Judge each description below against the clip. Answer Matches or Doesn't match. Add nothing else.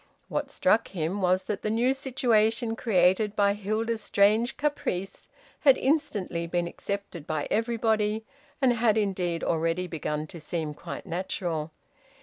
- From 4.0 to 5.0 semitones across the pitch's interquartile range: Matches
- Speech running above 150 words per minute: Doesn't match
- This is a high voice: Matches